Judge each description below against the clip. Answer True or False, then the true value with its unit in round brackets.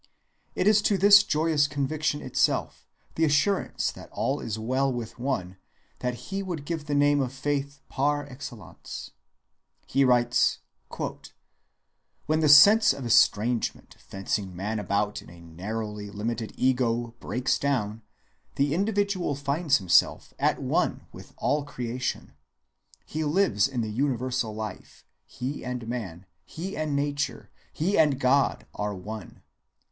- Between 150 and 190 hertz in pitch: False (130 Hz)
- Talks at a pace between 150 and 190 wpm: False (135 wpm)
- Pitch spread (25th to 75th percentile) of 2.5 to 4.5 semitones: False (4.9 semitones)